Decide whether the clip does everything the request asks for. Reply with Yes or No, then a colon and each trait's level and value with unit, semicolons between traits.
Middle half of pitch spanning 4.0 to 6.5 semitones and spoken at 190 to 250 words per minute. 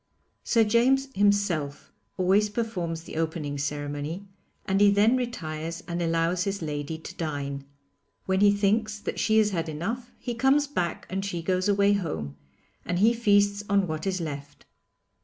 No: average, 4.4 semitones; average, 160 wpm